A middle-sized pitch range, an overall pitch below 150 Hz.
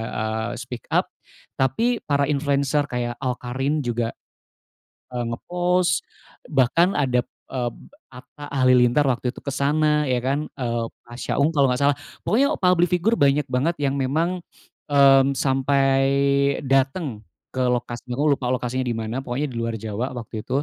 Yes: average, 3.1 semitones; low, 135 Hz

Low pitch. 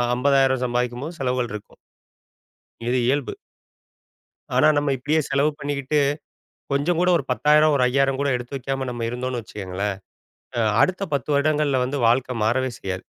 Yes: low, 130 Hz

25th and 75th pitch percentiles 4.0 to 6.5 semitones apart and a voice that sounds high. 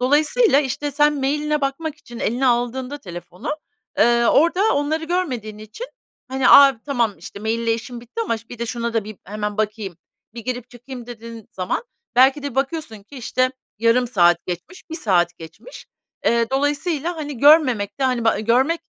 Yes: average, 4.5 semitones; very high, 250 Hz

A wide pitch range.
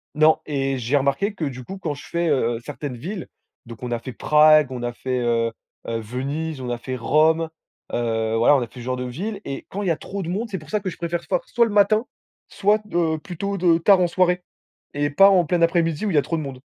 Yes: wide, 5.9 semitones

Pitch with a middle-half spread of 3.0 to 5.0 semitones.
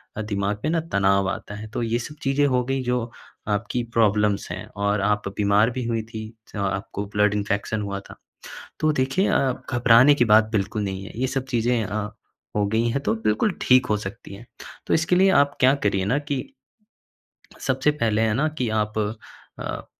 Yes: average, 4.0 semitones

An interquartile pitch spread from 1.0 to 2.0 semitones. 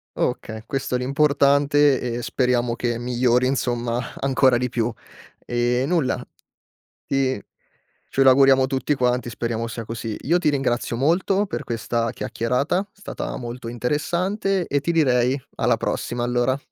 No: average, 2.8 semitones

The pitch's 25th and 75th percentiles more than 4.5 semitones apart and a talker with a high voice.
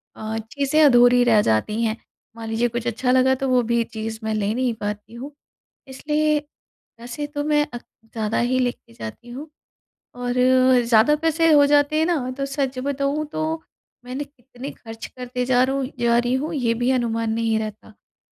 No: average, 3.5 semitones; high, 245 Hz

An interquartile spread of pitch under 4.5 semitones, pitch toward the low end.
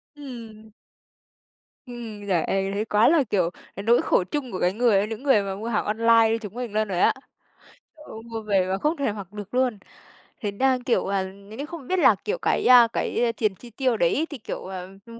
No: average, 3.7 semitones; high, 225 Hz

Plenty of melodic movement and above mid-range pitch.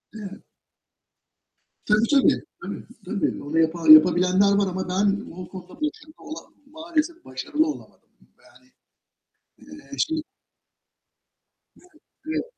Yes: wide, 9.0 semitones; high, 210 Hz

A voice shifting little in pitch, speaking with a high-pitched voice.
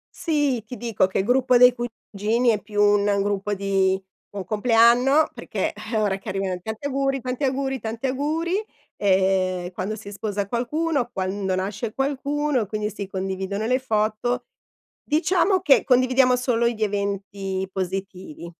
No: average, 4.6 semitones; high, 220 Hz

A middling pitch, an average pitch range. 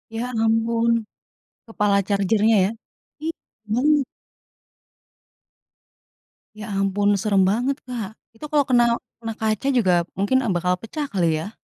No: high, 220 Hz; average, 3.4 semitones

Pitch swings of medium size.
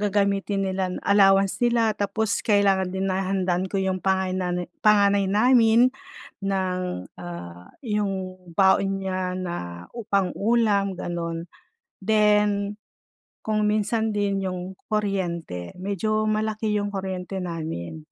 No: narrow, 2.3 semitones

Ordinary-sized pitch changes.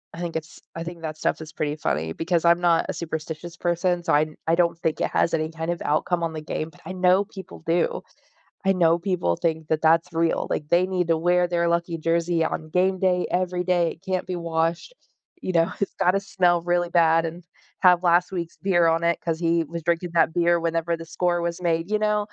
No: narrow, 1.4 semitones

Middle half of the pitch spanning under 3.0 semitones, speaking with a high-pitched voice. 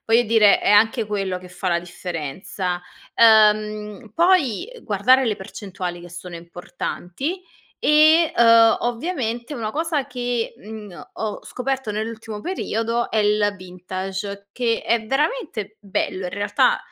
No: average, 4.1 semitones; high, 215 Hz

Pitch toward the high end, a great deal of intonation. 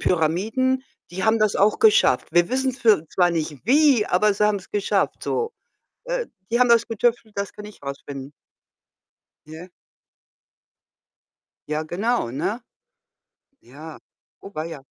Yes: high, 205 Hz; wide, 6.6 semitones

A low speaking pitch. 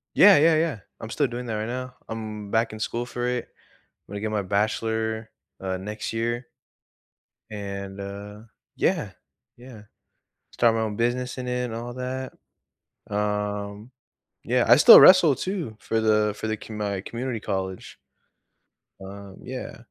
Yes: low, 110 Hz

